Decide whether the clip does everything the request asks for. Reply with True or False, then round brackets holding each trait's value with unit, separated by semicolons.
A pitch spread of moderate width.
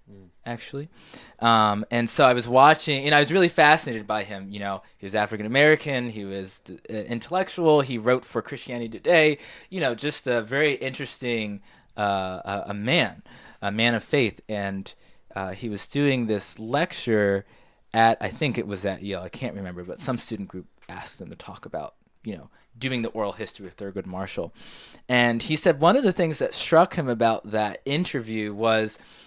False (5.7 semitones)